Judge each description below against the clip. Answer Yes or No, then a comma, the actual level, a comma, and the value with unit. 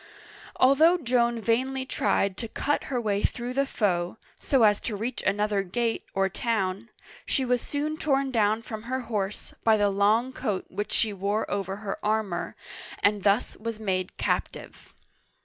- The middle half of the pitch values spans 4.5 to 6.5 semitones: No, average, 3.7 semitones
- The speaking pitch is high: Yes, high, 220 Hz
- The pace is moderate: Yes, average, 165 wpm